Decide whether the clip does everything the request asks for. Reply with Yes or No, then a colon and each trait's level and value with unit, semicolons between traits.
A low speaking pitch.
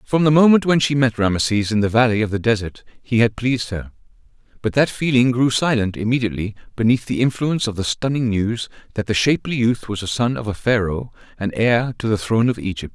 Yes: low, 115 Hz